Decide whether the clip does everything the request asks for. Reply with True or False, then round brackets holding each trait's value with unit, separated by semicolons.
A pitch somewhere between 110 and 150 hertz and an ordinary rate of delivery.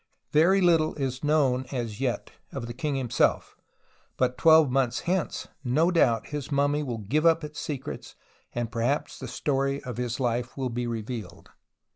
True (135 Hz; 165 wpm)